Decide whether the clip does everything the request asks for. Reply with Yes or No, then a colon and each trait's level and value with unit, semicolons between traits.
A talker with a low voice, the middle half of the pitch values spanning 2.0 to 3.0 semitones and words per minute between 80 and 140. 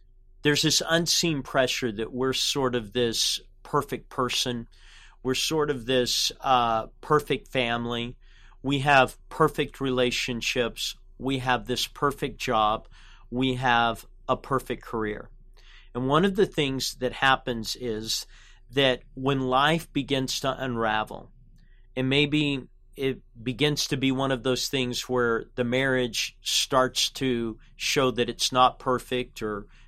Yes: low, 125 Hz; narrow, 2.4 semitones; slow, 135 wpm